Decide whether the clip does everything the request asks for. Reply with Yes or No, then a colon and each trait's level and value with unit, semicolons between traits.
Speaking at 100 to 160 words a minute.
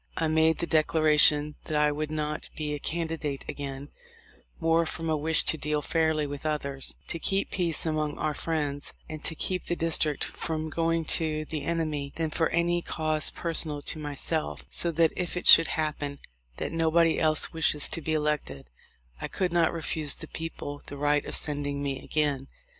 No: average, 185 wpm